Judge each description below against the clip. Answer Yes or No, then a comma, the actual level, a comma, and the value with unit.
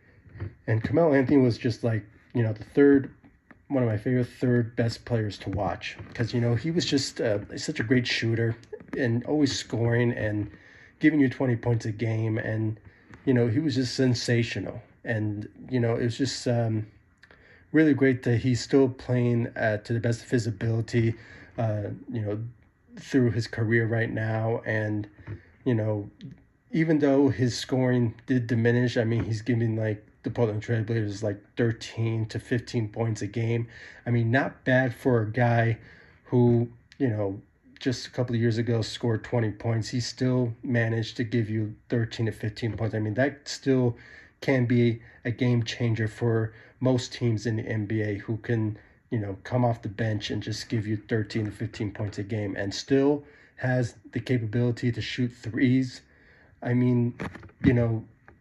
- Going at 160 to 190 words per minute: Yes, average, 180 wpm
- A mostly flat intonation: Yes, narrow, 2.3 semitones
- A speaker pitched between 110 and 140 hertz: Yes, low, 115 Hz